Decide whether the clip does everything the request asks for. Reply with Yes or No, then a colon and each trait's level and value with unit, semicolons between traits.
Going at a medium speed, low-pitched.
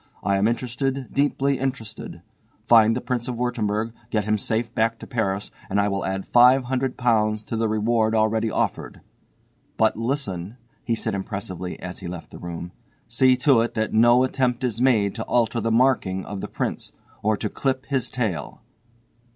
Yes: average, 175 wpm; low, 115 Hz